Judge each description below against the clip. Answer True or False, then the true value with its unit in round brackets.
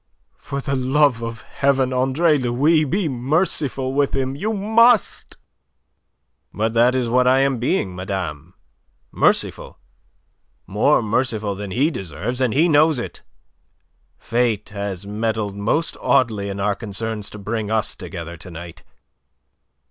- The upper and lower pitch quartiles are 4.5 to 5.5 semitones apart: True (5.2 semitones)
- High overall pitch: False (120 Hz)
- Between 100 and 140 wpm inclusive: True (135 wpm)